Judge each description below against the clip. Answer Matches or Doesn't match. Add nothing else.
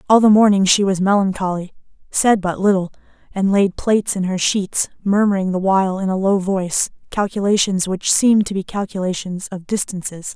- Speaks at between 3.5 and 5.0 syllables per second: Doesn't match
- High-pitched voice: Matches